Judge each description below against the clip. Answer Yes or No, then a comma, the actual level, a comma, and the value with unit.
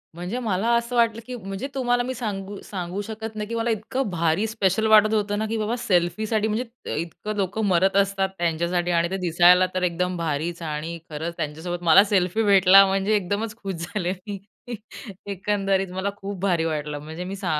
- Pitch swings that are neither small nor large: Yes, average, 3.7 semitones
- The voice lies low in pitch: No, high, 195 Hz